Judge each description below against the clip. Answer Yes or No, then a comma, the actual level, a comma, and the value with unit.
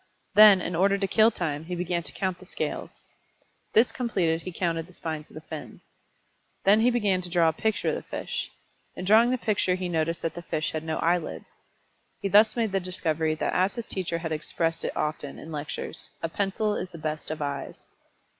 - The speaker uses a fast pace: Yes, fast, 210 wpm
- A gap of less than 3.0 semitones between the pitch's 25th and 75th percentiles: No, average, 3.7 semitones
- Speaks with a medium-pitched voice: Yes, medium, 175 Hz